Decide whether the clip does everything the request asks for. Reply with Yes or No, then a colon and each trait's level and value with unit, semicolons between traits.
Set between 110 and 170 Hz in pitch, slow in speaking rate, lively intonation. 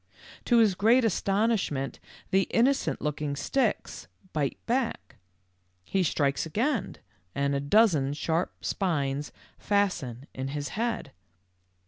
No: medium, 180 Hz; slow, 115 wpm; wide, 7.9 semitones